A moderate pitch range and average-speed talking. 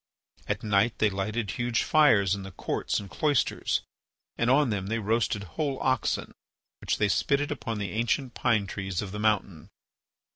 Yes: average, 3.4 semitones; average, 170 wpm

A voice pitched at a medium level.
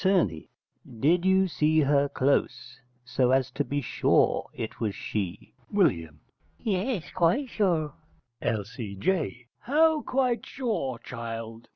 Yes: medium, 145 Hz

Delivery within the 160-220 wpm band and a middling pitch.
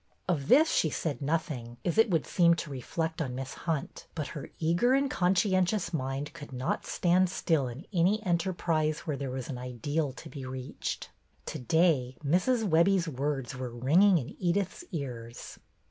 Yes: average, 170 wpm; medium, 160 Hz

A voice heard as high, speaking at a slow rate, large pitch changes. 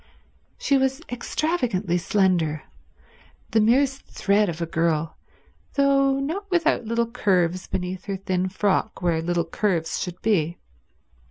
Yes: high, 195 Hz; slow, 125 wpm; wide, 7.3 semitones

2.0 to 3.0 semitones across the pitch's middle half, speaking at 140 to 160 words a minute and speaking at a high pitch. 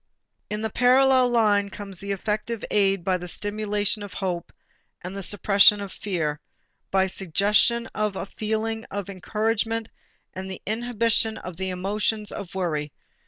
Yes: narrow, 2.5 semitones; average, 150 wpm; high, 205 Hz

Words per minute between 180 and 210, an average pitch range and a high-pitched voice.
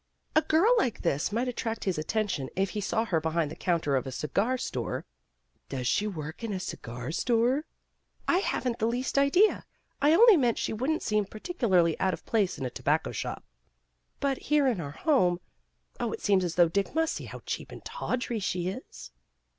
No: average, 200 wpm; wide, 7.5 semitones; high, 210 Hz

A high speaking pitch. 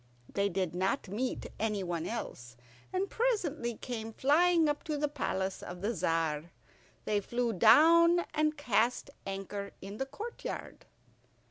Yes: high, 230 Hz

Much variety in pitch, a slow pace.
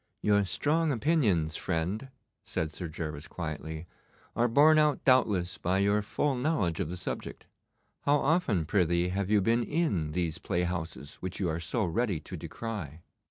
No: wide, 6.6 semitones; average, 160 wpm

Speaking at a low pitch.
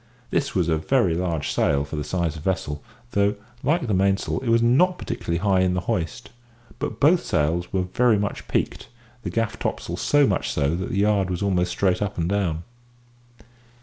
Yes: very low, 95 Hz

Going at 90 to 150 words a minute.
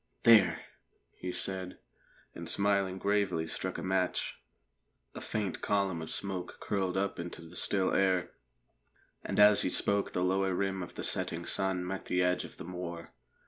No: average, 165 wpm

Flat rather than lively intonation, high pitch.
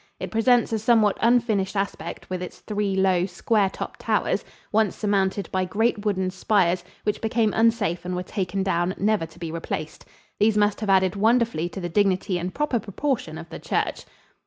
No: average, 3.2 semitones; high, 200 Hz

